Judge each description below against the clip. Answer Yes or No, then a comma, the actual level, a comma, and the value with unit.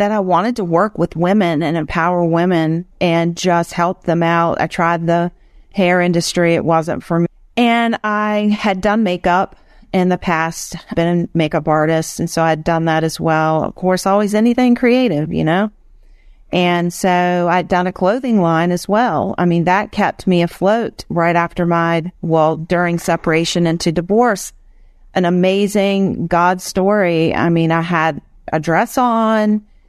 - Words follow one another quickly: No, average, 170 wpm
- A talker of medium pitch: Yes, medium, 175 Hz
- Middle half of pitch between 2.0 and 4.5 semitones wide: Yes, average, 3.0 semitones